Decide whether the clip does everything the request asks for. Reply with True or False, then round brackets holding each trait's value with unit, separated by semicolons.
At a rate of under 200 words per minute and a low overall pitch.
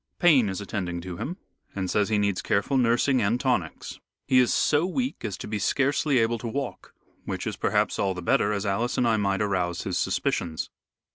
False (205 wpm; 105 Hz)